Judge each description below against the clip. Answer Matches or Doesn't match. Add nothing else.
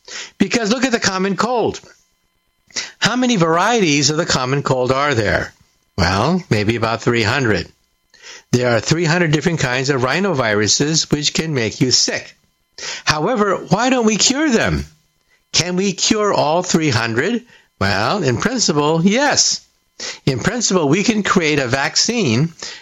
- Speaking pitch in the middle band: Matches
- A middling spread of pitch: Doesn't match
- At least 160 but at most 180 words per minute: Doesn't match